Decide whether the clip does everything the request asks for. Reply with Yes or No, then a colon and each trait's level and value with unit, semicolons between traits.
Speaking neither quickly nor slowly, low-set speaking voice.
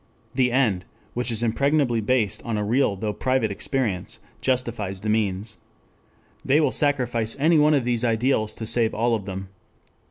Yes: average, 165 wpm; low, 115 Hz